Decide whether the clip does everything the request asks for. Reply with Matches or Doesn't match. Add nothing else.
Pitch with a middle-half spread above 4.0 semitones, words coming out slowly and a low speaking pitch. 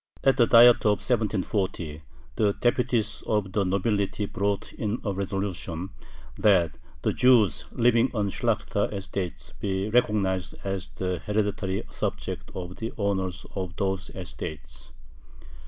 Doesn't match